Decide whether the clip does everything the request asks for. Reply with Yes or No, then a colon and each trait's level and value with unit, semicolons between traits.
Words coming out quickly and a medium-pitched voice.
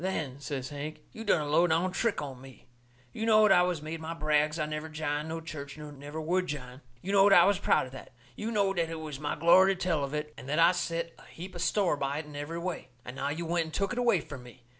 Yes: fast, 275 wpm; medium, 160 Hz